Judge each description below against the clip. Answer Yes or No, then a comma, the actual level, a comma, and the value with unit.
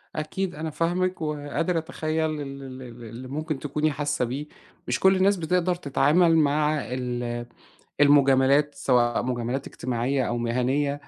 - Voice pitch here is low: No, medium, 145 Hz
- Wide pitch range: No, average, 3.5 semitones